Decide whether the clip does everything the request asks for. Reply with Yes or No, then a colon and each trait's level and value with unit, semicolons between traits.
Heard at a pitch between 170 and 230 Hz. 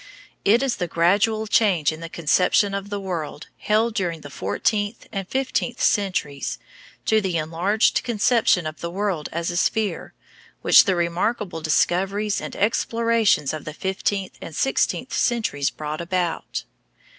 Yes: high, 190 Hz